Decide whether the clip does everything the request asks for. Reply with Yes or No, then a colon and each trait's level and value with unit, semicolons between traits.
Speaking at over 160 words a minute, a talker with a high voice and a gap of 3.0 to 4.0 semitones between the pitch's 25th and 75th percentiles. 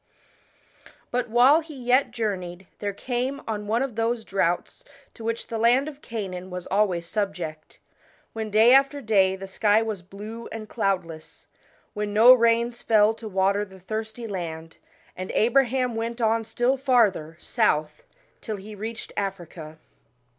No: average, 150 wpm; high, 215 Hz; average, 3.7 semitones